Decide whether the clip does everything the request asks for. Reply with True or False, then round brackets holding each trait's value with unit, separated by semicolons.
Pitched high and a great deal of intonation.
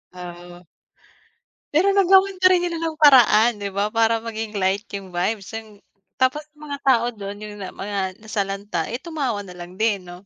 True (215 Hz; 5.7 semitones)